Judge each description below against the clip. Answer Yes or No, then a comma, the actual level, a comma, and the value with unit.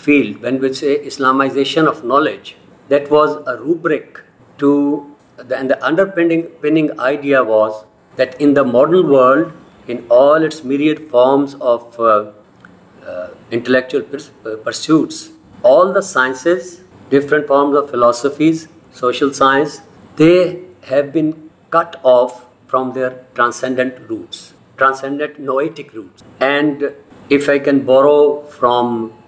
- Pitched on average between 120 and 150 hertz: Yes, medium, 140 Hz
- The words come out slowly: Yes, slow, 130 wpm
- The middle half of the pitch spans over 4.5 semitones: No, average, 3.3 semitones